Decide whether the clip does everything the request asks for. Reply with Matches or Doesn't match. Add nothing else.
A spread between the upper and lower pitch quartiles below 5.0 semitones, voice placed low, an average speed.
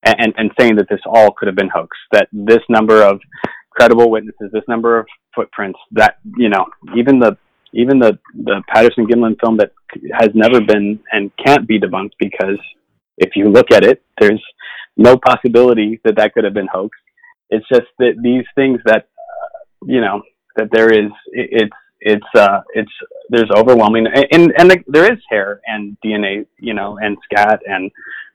Matches